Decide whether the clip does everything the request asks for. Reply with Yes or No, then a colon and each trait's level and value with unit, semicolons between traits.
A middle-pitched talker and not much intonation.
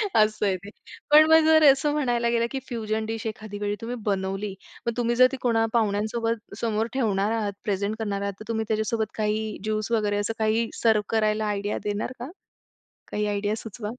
No: high, 220 Hz; narrow, 1.9 semitones